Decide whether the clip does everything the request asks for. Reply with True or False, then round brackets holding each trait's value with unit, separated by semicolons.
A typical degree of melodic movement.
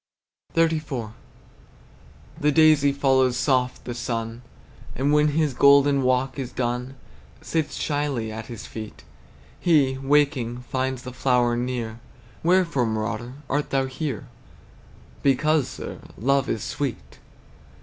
True (3.1 semitones)